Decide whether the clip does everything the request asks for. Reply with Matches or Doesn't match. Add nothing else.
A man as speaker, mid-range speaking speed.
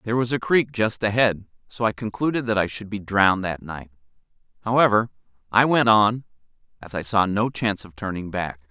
Matches